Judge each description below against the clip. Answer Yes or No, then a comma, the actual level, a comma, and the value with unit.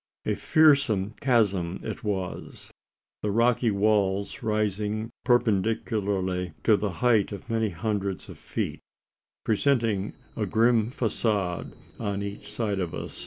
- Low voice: Yes, low, 105 Hz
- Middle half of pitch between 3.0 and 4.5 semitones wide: No, narrow, 2.6 semitones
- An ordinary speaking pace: No, slow, 120 wpm